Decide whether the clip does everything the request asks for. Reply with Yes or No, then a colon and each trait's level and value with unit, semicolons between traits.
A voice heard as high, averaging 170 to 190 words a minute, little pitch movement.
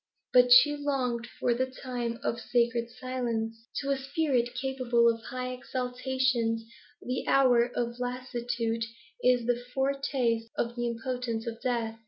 No: high, 245 Hz; average, 140 wpm; narrow, 1.6 semitones